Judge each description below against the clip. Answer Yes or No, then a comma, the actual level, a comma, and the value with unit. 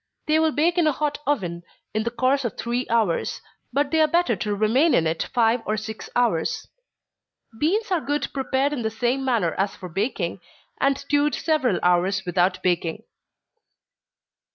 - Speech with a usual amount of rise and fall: No, wide, 6.9 semitones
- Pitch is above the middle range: Yes, high, 240 Hz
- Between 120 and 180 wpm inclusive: Yes, average, 175 wpm